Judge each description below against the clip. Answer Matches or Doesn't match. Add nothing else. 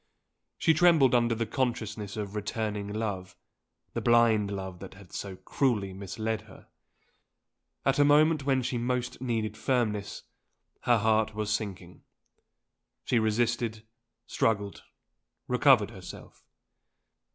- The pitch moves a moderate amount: Matches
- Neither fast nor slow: Doesn't match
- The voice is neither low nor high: Doesn't match